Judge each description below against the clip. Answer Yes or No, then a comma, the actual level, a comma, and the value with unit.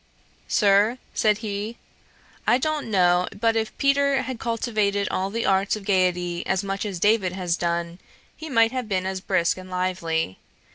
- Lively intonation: No, average, 3.7 semitones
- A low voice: No, high, 200 Hz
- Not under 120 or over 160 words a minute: No, average, 170 wpm